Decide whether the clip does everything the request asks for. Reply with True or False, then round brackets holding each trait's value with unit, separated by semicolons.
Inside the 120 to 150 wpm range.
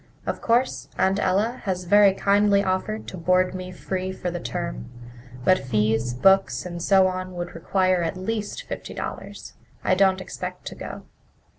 False (165 wpm)